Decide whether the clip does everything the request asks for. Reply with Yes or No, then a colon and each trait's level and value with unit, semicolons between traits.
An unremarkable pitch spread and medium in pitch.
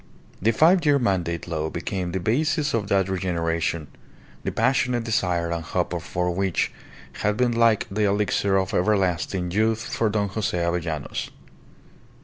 No: average, 4.4 semitones; very low, 95 Hz